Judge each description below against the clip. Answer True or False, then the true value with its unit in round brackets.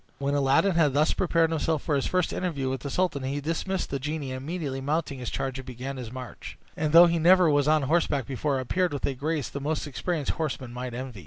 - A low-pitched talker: False (145 Hz)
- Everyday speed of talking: False (230 wpm)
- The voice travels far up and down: False (3.5 semitones)